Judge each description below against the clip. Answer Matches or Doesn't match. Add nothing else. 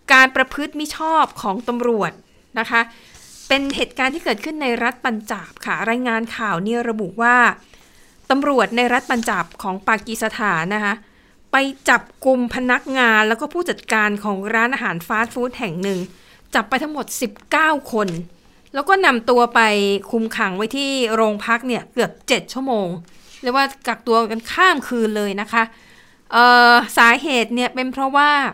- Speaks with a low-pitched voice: Doesn't match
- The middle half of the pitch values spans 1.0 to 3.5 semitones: Matches